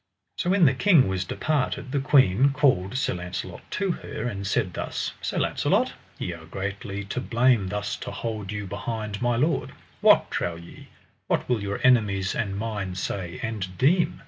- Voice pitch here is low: Yes, low, 105 Hz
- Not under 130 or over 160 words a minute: No, average, 175 wpm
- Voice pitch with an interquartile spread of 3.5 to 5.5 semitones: Yes, average, 5.1 semitones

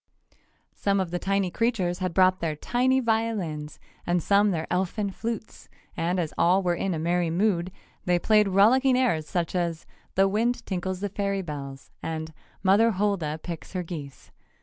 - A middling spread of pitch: Yes, average, 3.3 semitones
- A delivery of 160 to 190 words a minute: Yes, average, 170 wpm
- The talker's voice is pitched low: No, medium, 185 Hz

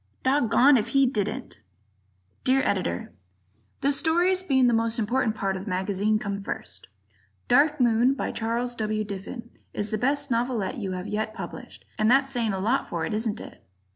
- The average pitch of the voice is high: Yes, high, 230 Hz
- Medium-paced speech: Yes, average, 175 wpm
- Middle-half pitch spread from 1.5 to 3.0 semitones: No, average, 4.2 semitones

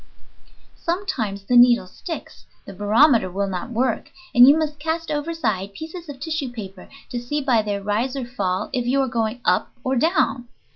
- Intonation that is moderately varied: No, wide, 6.1 semitones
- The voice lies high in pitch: Yes, high, 245 Hz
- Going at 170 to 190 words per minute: Yes, average, 180 wpm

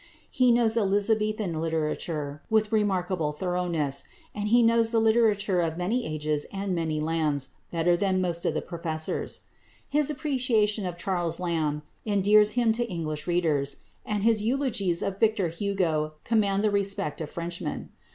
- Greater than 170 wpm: No, average, 150 wpm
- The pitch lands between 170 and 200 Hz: Yes, high, 190 Hz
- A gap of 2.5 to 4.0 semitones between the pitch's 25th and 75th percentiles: No, average, 4.8 semitones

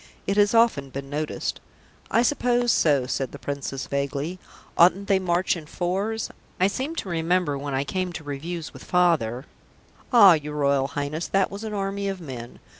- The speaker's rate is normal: Yes, average, 190 wpm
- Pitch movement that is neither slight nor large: No, wide, 5.7 semitones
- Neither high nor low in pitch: Yes, medium, 170 Hz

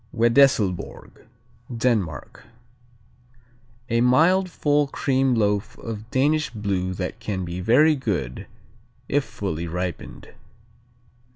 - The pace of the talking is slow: Yes, slow, 95 wpm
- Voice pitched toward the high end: No, low, 115 Hz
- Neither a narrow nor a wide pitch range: No, wide, 6.6 semitones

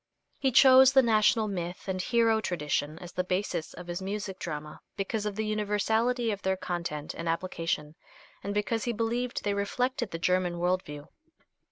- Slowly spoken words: No, average, 175 wpm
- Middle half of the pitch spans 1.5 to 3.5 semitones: No, average, 4.4 semitones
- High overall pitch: Yes, high, 195 Hz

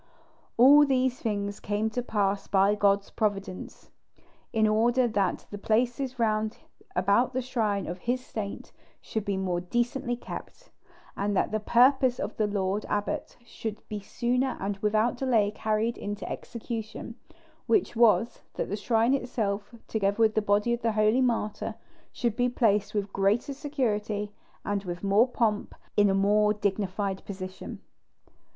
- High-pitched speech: Yes, high, 215 Hz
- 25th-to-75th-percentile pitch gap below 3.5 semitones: Yes, average, 2.9 semitones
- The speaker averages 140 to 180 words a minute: Yes, average, 150 wpm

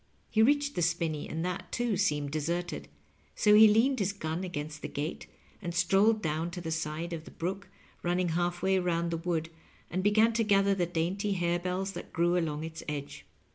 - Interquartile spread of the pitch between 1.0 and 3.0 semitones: No, average, 3.4 semitones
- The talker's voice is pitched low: No, medium, 175 Hz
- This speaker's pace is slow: No, average, 190 wpm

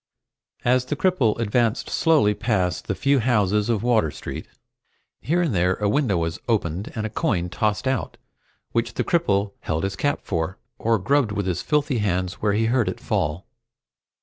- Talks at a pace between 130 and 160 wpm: No, average, 175 wpm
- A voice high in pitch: No, low, 105 Hz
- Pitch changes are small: No, average, 5.1 semitones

